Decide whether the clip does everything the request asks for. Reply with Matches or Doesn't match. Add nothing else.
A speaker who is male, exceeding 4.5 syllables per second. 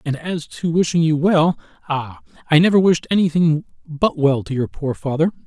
Matches